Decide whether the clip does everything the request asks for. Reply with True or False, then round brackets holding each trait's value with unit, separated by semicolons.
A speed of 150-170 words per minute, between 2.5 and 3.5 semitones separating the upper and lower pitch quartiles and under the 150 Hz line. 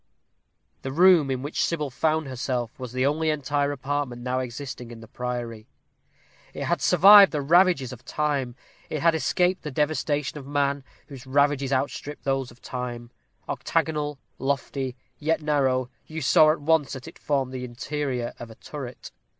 True (165 wpm; 2.8 semitones; 140 Hz)